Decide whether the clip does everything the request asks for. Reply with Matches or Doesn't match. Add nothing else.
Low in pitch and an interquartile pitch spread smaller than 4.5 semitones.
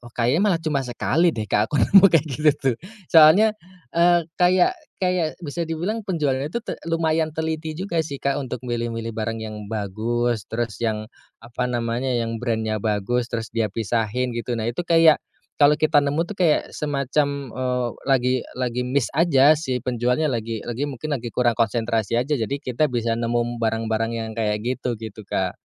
Doesn't match